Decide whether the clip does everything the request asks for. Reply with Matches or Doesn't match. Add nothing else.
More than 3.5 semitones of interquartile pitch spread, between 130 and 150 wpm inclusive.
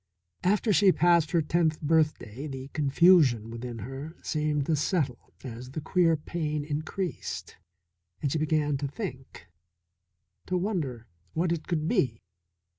Matches